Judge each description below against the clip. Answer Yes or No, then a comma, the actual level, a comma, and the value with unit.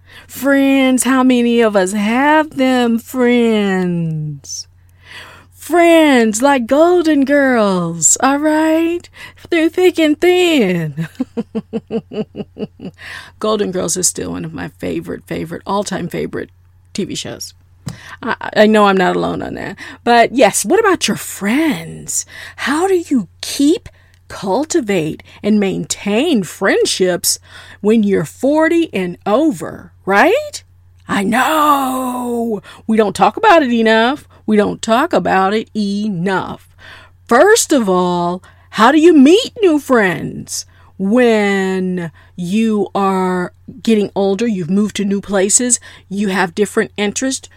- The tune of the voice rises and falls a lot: Yes, wide, 6.6 semitones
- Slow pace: Yes, slow, 120 wpm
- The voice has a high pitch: Yes, high, 215 Hz